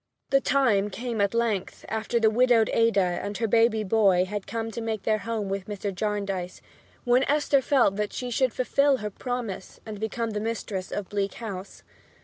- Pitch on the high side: Yes, high, 220 Hz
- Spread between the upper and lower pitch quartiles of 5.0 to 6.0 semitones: No, average, 2.8 semitones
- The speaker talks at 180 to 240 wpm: Yes, average, 185 wpm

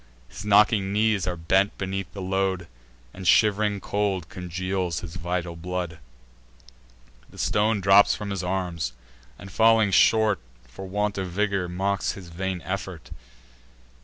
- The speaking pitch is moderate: No, very low, 95 Hz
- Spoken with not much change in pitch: Yes, narrow, 2.2 semitones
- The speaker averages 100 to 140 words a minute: Yes, slow, 135 wpm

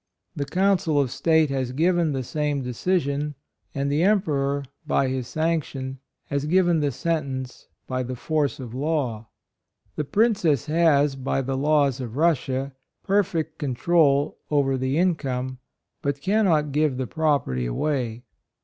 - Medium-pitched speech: Yes, medium, 145 Hz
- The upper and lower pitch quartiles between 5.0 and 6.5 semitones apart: No, average, 3.4 semitones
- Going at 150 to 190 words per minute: No, average, 140 wpm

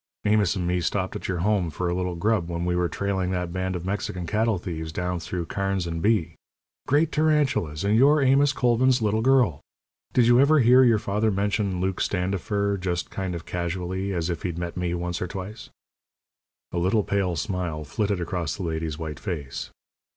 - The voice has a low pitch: Yes, very low, 95 Hz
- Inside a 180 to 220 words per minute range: Yes, average, 195 wpm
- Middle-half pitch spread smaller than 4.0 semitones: Yes, average, 3.6 semitones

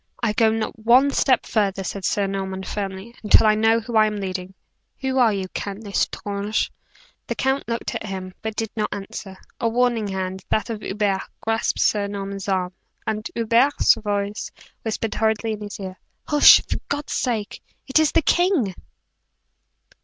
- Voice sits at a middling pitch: No, high, 215 Hz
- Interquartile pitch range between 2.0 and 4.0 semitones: Yes, average, 2.7 semitones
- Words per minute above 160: Yes, average, 170 wpm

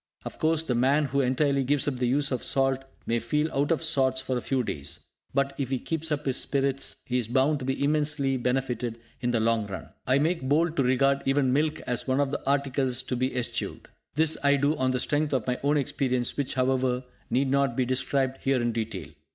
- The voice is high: No, low, 135 Hz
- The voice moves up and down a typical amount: No, narrow, 2.2 semitones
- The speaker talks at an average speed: No, fast, 225 wpm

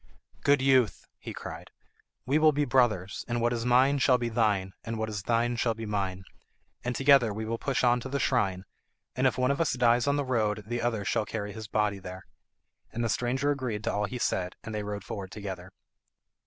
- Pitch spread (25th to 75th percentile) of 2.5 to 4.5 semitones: Yes, average, 3.6 semitones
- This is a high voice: No, low, 115 Hz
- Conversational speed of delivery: No, fast, 220 wpm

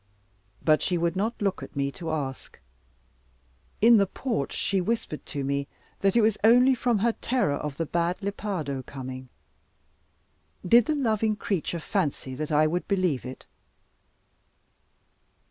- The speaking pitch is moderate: Yes, medium, 180 Hz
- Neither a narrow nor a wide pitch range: No, wide, 6.9 semitones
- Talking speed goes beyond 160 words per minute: No, average, 145 wpm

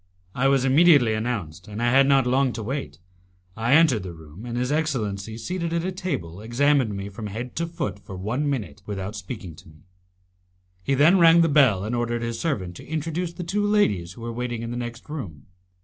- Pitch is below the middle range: Yes, low, 120 Hz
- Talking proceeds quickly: Yes, fast, 210 wpm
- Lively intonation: Yes, wide, 6.4 semitones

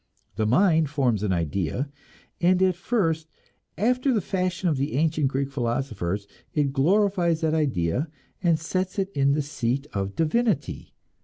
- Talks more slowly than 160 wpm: Yes, average, 150 wpm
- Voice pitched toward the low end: No, medium, 150 Hz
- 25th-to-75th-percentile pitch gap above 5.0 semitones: Yes, wide, 5.6 semitones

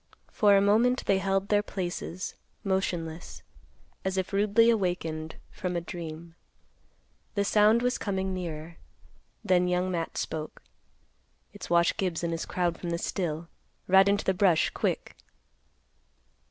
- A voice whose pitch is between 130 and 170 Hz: No, medium, 185 Hz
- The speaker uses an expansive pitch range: No, average, 2.8 semitones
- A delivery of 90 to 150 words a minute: Yes, average, 140 wpm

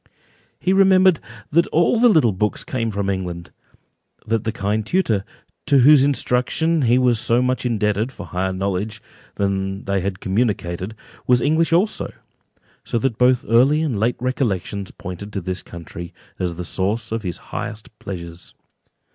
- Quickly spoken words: No, average, 155 wpm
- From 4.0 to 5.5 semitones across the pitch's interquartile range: Yes, average, 4.9 semitones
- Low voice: Yes, low, 110 Hz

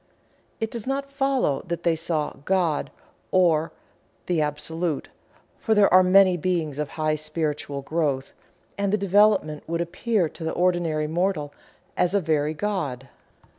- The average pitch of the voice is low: No, medium, 170 Hz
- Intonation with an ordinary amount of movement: Yes, average, 3.9 semitones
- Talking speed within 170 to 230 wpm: No, average, 145 wpm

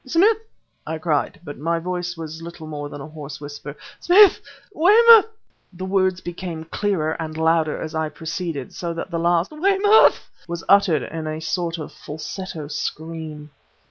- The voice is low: No, medium, 165 Hz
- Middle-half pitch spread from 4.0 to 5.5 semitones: No, average, 3.2 semitones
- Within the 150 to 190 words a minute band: Yes, average, 160 wpm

